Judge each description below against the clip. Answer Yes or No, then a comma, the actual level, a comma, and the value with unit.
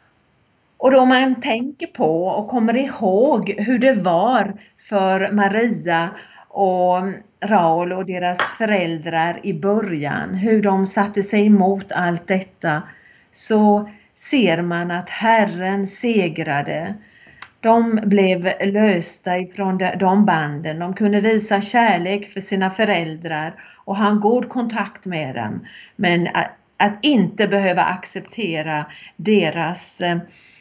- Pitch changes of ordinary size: Yes, average, 3.3 semitones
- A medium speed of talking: No, slow, 120 wpm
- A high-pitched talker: Yes, high, 195 Hz